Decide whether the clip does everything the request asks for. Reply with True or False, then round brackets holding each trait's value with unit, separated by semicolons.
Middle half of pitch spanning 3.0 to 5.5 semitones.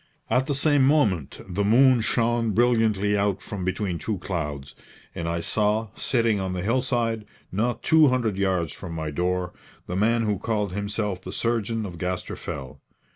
True (4.2 semitones)